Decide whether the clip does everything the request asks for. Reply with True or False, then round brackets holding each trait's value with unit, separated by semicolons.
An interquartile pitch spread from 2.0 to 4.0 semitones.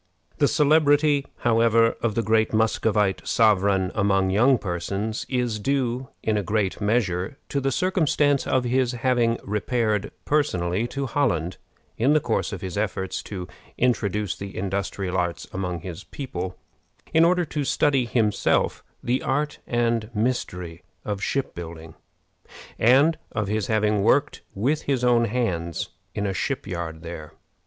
False (5.1 semitones)